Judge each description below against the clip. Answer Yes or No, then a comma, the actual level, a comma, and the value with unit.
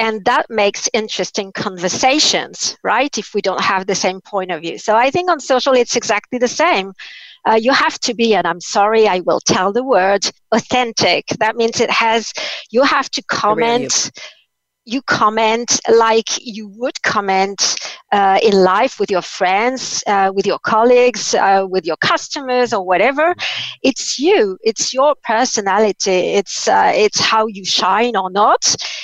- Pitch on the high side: Yes, high, 220 Hz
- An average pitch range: Yes, average, 4.3 semitones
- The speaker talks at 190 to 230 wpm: No, average, 165 wpm